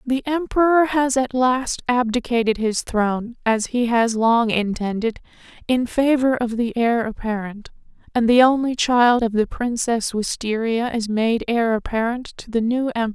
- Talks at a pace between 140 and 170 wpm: Yes, average, 160 wpm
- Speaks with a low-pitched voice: No, high, 235 Hz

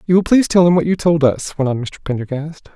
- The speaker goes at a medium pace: No, fast, 285 wpm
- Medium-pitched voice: Yes, medium, 160 Hz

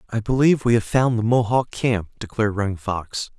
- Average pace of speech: Yes, average, 195 wpm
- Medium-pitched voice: No, low, 110 Hz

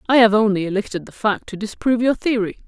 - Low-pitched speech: No, high, 215 Hz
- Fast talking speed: Yes, fast, 225 wpm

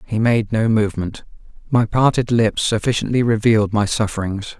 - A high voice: No, low, 110 Hz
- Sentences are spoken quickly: No, average, 145 wpm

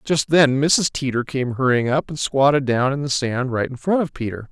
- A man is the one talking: Yes, male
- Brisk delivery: Yes, fast, 240 wpm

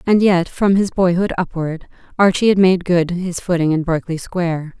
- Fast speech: No, average, 190 wpm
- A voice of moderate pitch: Yes, medium, 175 Hz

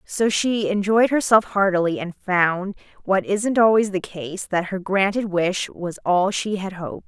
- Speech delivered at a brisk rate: No, average, 180 wpm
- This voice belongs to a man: No, female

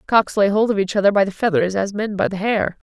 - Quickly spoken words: Yes, fast, 290 wpm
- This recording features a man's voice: No, female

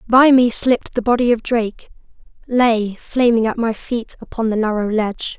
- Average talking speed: Yes, average, 180 wpm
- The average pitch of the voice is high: Yes, high, 230 Hz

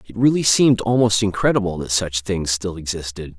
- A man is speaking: Yes, male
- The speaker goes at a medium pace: Yes, average, 175 wpm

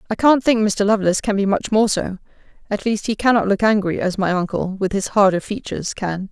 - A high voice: Yes, high, 205 Hz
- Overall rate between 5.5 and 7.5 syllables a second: Yes, 5.9 syllables/s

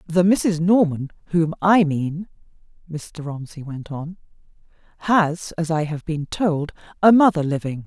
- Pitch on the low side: No, medium, 165 Hz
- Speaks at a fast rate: No, average, 145 wpm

